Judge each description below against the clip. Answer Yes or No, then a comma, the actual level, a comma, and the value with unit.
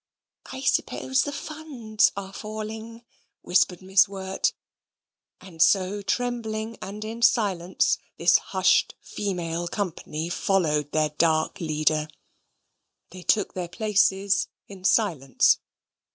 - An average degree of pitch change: Yes, average, 4.0 semitones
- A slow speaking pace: Yes, slow, 110 wpm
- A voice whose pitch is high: Yes, high, 195 Hz